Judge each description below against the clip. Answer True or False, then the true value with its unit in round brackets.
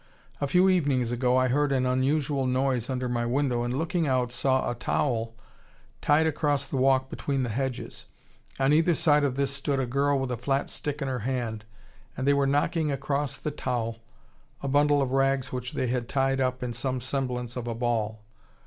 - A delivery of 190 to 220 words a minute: True (200 wpm)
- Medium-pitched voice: False (130 Hz)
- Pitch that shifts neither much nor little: False (2.3 semitones)